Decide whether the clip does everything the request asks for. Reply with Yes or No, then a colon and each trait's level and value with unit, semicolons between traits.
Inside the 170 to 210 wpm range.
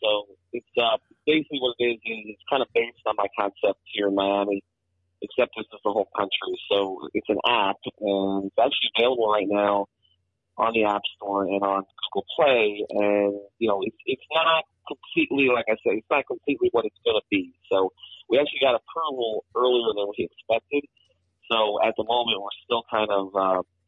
Yes: average, 195 wpm